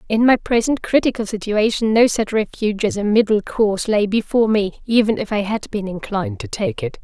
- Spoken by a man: No, female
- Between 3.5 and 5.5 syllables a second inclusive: No, 5.7 syllables/s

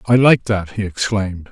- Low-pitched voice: Yes, low, 105 Hz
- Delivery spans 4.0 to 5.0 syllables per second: No, 5.3 syllables/s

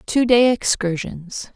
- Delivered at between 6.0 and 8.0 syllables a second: No, 3.5 syllables/s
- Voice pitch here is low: No, high, 215 Hz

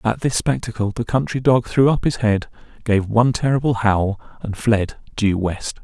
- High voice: No, low, 115 Hz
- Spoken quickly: No, average, 185 wpm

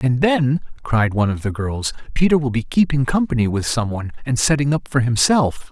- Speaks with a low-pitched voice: Yes, low, 130 Hz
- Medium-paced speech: No, fast, 210 wpm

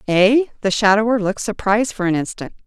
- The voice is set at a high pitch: Yes, high, 210 Hz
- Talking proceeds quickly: No, average, 180 wpm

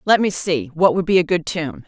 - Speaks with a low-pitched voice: No, medium, 175 Hz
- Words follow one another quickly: Yes, fast, 290 wpm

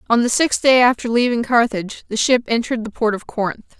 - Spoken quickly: Yes, fast, 220 wpm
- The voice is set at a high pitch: Yes, high, 230 Hz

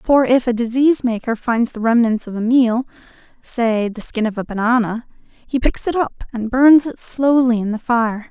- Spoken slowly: No, average, 200 wpm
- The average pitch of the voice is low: No, high, 240 Hz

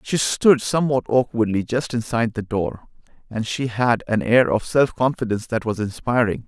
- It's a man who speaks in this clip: Yes, male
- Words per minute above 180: No, average, 175 wpm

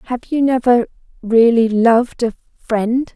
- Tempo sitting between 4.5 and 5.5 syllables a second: No, 4.2 syllables/s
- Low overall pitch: No, high, 235 Hz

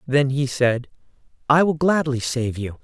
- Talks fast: No, average, 170 wpm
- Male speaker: Yes, male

